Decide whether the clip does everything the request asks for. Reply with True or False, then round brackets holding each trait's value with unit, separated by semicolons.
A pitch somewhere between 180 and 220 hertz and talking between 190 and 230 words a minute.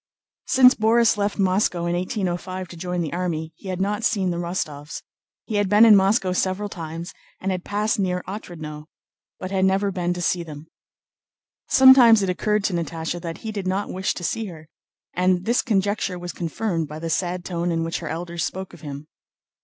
True (185 Hz; 195 wpm)